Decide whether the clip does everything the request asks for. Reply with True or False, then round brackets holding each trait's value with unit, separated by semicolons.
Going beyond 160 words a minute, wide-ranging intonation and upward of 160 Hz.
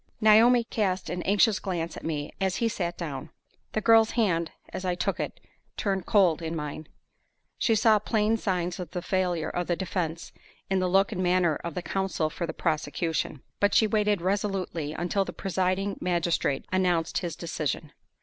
False (180 wpm; 3.2 semitones; 185 Hz)